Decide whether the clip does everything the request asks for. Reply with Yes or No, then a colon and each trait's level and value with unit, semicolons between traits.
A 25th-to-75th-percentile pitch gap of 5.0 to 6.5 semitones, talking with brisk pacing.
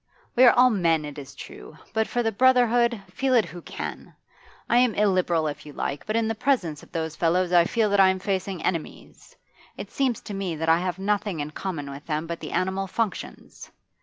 Yes: wide, 5.4 semitones; fast, 220 wpm